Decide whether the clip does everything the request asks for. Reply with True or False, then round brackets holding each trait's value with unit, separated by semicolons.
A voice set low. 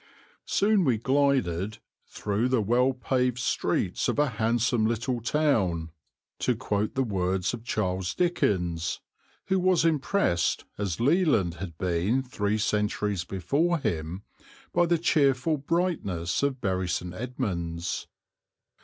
True (115 Hz)